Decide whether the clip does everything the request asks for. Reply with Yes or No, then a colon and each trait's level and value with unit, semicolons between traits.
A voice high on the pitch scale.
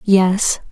Yes: high, 195 Hz